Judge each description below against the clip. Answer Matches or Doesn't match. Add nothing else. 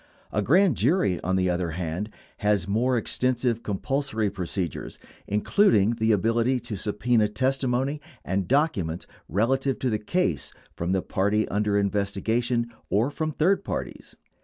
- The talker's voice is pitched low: Matches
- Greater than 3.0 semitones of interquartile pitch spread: Matches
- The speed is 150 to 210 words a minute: Doesn't match